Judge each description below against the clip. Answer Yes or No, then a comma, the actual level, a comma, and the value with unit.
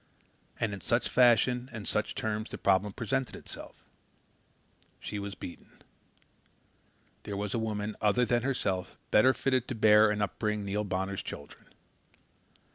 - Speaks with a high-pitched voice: No, low, 105 Hz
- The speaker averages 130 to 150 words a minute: Yes, average, 140 wpm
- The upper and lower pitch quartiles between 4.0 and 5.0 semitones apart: No, average, 2.9 semitones